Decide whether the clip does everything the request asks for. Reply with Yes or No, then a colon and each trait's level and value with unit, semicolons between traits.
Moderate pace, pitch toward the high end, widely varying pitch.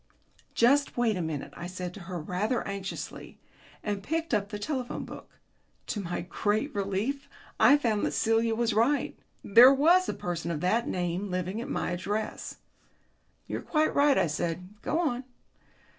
Yes: average, 165 wpm; high, 210 Hz; wide, 5.8 semitones